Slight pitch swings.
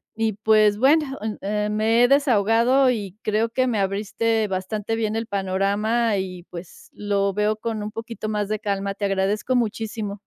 Yes: narrow, 2.2 semitones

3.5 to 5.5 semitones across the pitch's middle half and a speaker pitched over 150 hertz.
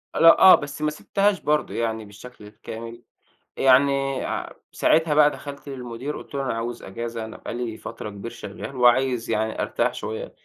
No: average, 3.9 semitones; low, 125 Hz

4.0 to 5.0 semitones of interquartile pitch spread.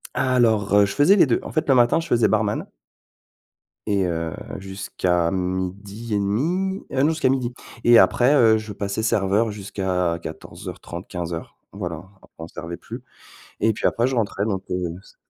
Yes: average, 4.5 semitones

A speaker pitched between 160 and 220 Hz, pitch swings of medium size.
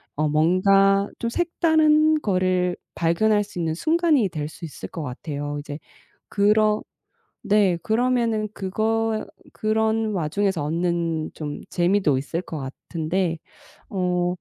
Yes: high, 190 Hz; average, 4.9 semitones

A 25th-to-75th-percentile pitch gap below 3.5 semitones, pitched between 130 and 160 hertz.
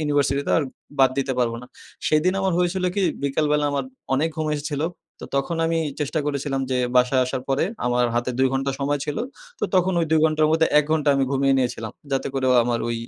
Yes: average, 2.8 semitones; medium, 140 Hz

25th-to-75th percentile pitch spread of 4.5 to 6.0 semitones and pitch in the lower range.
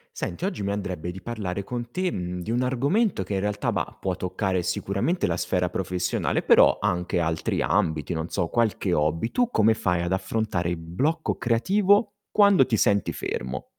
Yes: average, 5.2 semitones; low, 100 Hz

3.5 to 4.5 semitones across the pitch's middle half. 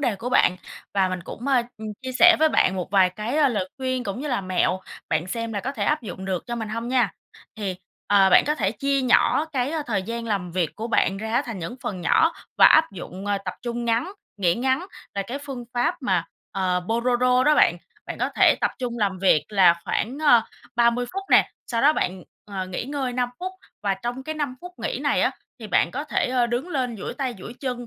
No: average, 5.0 semitones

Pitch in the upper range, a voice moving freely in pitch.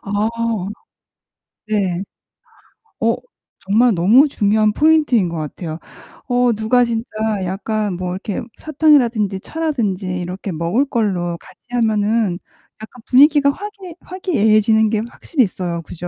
No: high, 215 Hz; average, 4.7 semitones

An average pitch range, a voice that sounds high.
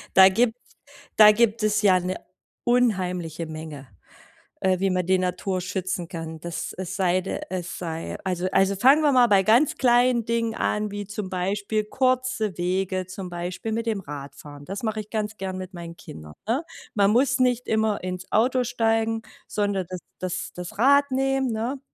Yes: average, 3.9 semitones; high, 200 Hz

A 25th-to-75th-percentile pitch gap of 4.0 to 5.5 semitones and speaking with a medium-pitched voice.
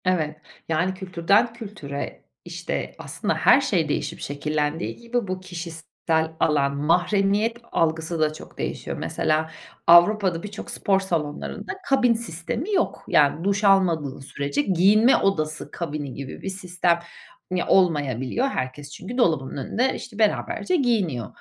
Yes: average, 5.0 semitones; medium, 175 Hz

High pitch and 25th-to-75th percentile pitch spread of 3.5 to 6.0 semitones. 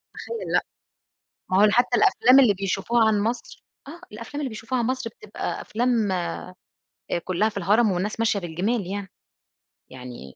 Yes: high, 215 Hz; average, 3.8 semitones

